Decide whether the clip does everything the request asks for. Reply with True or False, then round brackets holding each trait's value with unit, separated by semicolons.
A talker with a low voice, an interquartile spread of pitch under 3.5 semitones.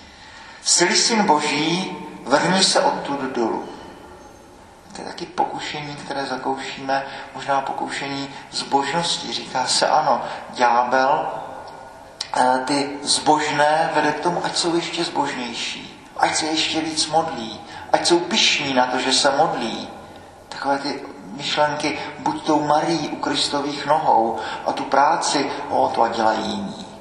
False (150 Hz; 2.7 semitones)